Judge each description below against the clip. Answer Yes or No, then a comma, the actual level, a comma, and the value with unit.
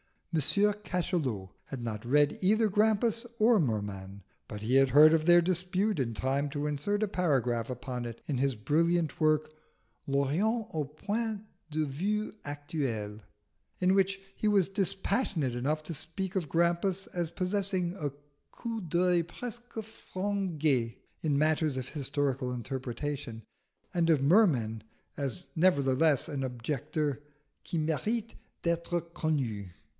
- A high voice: No, medium, 155 Hz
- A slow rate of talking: Yes, slow, 130 wpm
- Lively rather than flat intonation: Yes, wide, 5.9 semitones